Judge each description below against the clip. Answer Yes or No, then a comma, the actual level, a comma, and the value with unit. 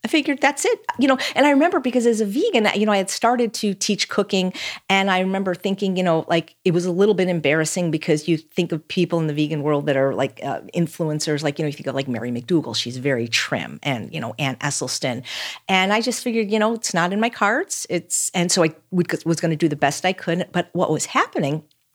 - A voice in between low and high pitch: Yes, medium, 175 Hz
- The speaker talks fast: Yes, fast, 255 wpm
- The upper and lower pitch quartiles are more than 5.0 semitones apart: Yes, wide, 5.4 semitones